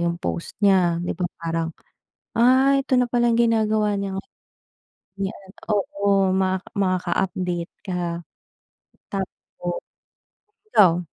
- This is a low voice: No, high, 190 Hz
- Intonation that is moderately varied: Yes, average, 3.0 semitones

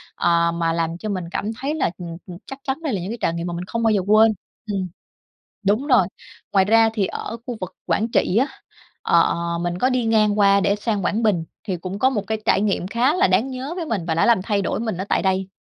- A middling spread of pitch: Yes, average, 4.3 semitones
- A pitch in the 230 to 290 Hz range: No, high, 205 Hz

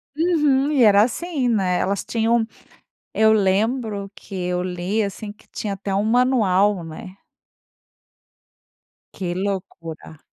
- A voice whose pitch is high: Yes, high, 205 Hz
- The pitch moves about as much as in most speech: Yes, average, 3.9 semitones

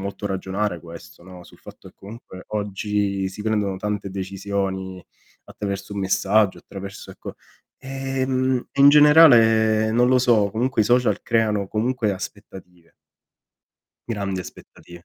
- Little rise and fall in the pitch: No, average, 3.3 semitones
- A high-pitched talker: No, low, 105 Hz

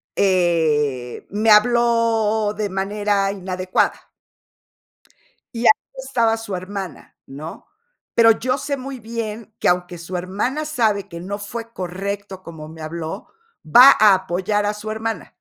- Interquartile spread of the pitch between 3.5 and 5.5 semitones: Yes, average, 3.8 semitones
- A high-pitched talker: Yes, high, 205 Hz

